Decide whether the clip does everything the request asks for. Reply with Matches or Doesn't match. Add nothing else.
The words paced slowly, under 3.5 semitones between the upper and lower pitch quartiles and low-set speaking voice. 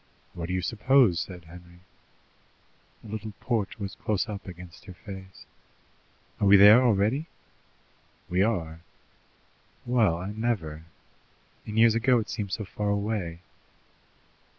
Doesn't match